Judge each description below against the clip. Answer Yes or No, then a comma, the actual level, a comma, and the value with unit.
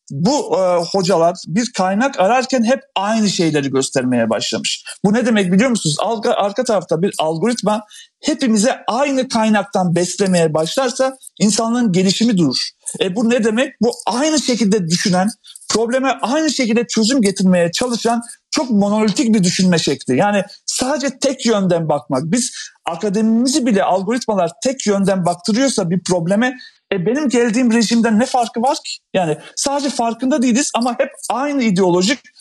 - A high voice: Yes, high, 225 Hz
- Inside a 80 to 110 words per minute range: No, fast, 145 wpm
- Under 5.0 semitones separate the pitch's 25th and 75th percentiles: No, average, 5.3 semitones